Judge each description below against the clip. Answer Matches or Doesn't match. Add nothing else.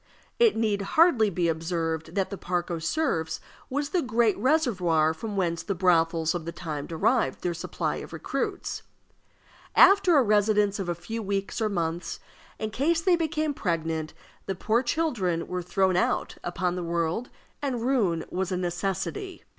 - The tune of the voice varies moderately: Doesn't match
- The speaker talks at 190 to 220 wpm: Doesn't match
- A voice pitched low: Doesn't match